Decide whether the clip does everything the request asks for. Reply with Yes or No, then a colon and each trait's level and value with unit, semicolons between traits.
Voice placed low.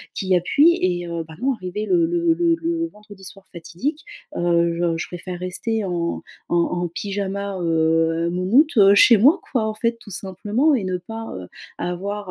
No: high, 195 Hz